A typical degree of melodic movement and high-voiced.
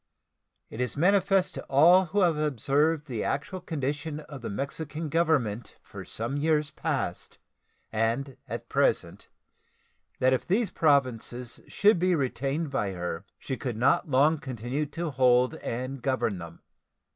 No: average, 4.3 semitones; medium, 140 Hz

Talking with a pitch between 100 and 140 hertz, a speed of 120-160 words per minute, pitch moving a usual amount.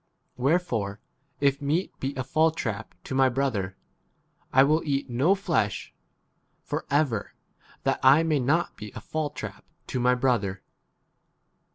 Yes: low, 135 Hz; average, 150 wpm; average, 4.4 semitones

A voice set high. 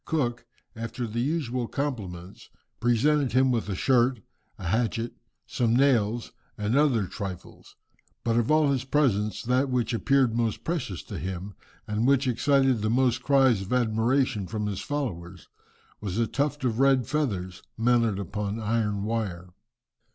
No: low, 115 Hz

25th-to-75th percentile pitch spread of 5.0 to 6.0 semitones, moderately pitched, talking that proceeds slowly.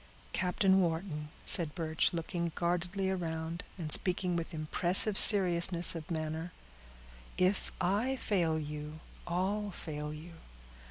No: average, 2.8 semitones; medium, 170 Hz; slow, 115 wpm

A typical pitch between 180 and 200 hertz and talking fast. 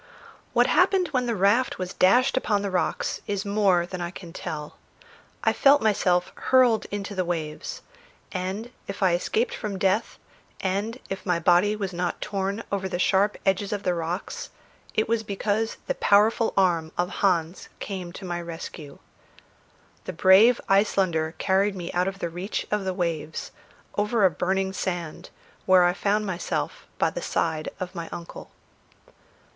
No: high, 190 Hz; average, 165 wpm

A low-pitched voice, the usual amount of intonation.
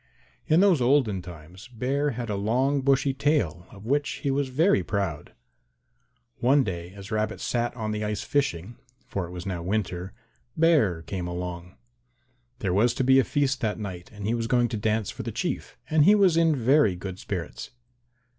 No: low, 110 Hz; wide, 6.5 semitones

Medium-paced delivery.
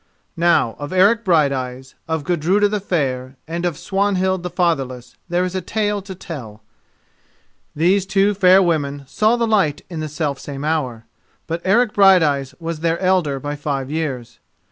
Yes: average, 165 wpm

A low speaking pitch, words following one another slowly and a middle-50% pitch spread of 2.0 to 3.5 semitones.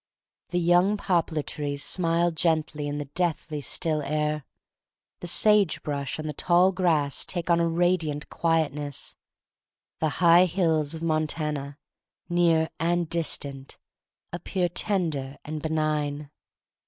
No: medium, 160 Hz; slow, 125 wpm; average, 2.7 semitones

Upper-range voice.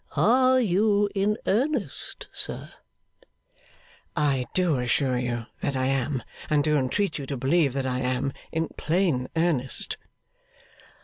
No: medium, 145 Hz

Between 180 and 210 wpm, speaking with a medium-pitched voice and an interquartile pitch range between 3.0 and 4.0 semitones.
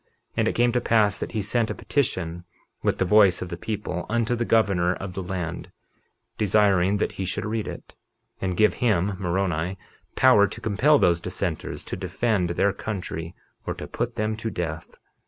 No: average, 190 wpm; low, 100 Hz; average, 3.6 semitones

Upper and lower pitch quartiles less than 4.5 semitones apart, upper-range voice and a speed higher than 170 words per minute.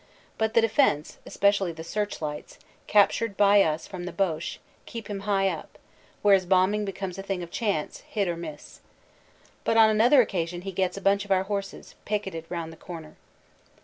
Yes: average, 3.1 semitones; high, 195 Hz; average, 185 wpm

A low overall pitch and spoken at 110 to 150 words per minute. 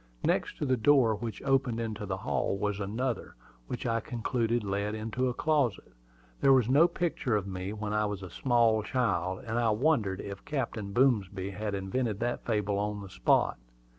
No: low, 110 Hz; average, 185 wpm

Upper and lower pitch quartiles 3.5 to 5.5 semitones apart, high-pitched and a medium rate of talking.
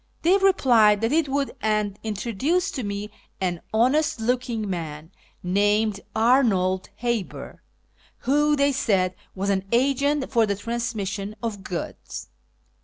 No: average, 4.9 semitones; high, 220 Hz; slow, 130 wpm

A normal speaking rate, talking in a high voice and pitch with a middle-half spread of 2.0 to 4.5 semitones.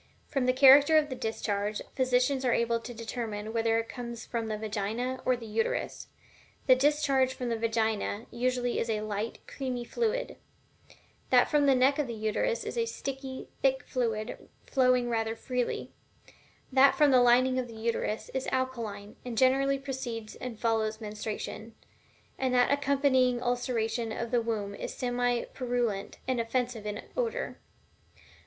Yes: average, 160 wpm; high, 245 Hz; average, 2.7 semitones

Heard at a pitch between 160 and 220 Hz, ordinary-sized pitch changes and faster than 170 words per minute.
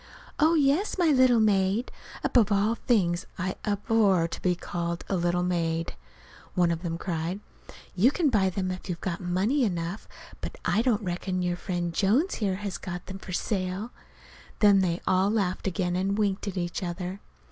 Yes: high, 190 Hz; average, 3.2 semitones; average, 180 wpm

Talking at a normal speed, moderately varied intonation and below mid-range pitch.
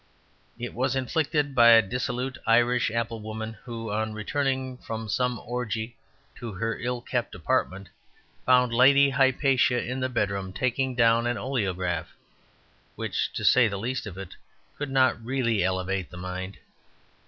Yes: average, 150 wpm; average, 3.1 semitones; low, 120 Hz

